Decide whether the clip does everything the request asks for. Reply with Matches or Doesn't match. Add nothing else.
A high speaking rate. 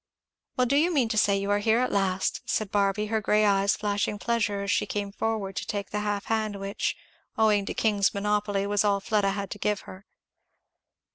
Matches